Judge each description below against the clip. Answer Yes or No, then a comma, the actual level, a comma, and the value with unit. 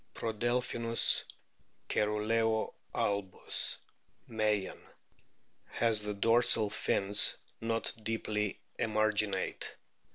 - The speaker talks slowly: Yes, slow, 65 wpm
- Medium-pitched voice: No, low, 110 Hz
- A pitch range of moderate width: No, narrow, 1.5 semitones